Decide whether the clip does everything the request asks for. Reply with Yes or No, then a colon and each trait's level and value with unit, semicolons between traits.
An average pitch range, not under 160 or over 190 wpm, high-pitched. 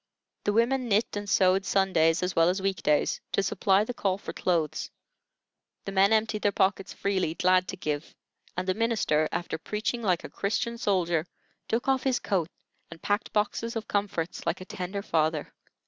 Yes: average, 3.2 semitones; average, 180 wpm; high, 195 Hz